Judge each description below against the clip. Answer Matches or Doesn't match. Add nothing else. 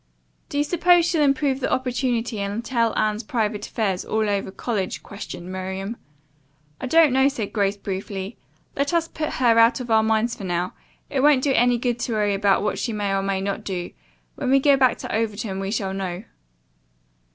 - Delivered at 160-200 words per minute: Matches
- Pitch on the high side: Matches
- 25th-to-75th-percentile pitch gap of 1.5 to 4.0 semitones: Doesn't match